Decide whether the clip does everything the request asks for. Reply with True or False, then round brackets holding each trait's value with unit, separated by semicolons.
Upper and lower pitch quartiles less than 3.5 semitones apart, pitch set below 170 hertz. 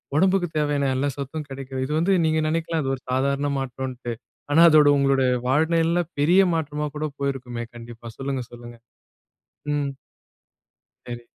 True (3.0 semitones; 140 Hz)